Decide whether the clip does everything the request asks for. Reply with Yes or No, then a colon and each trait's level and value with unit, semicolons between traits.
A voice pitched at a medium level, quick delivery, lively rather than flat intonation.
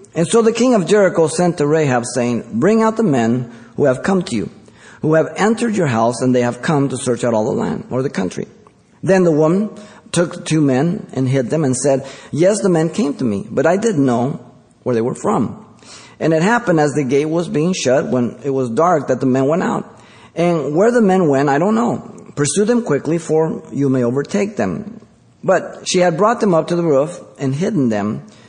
Yes: medium, 155 Hz; fast, 225 wpm; wide, 6.4 semitones